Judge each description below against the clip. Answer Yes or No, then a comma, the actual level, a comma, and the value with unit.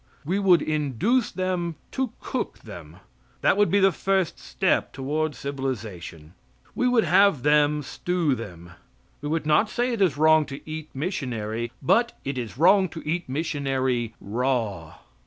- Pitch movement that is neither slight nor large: No, wide, 6.2 semitones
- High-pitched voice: No, medium, 150 Hz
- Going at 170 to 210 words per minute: No, average, 155 wpm